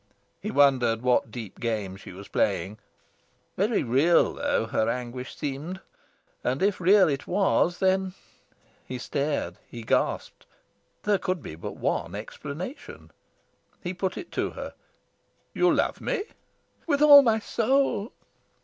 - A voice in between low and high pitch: Yes, medium, 150 Hz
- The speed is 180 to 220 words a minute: No, slow, 135 wpm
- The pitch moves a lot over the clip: Yes, wide, 8.6 semitones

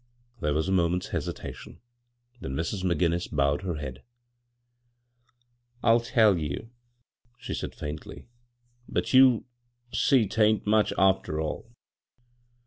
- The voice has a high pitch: No, very low, 95 Hz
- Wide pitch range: Yes, wide, 7.2 semitones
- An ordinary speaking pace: No, slow, 125 wpm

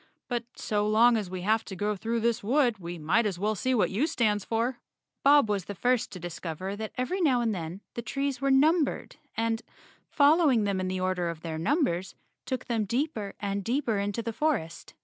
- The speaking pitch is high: Yes, high, 220 Hz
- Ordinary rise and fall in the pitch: Yes, average, 4.9 semitones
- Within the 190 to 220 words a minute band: Yes, fast, 205 wpm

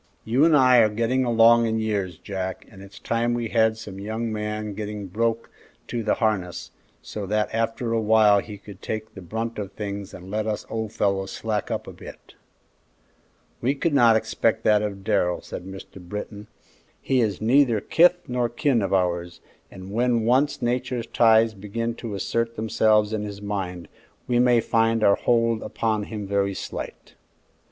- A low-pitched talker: Yes, low, 110 Hz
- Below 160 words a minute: No, average, 180 wpm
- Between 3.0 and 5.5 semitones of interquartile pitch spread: No, narrow, 2.4 semitones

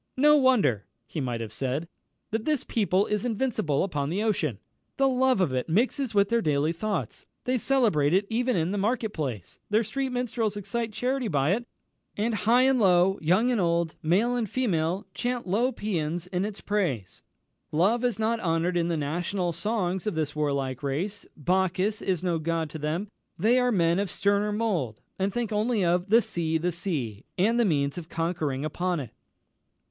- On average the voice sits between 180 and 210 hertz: Yes, high, 190 Hz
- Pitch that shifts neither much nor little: No, wide, 5.8 semitones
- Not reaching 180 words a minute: No, average, 185 wpm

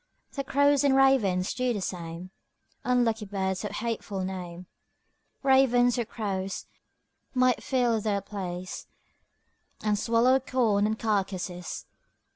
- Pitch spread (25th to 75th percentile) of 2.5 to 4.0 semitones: No, average, 4.7 semitones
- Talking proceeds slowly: Yes, slow, 115 wpm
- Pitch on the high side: Yes, high, 215 Hz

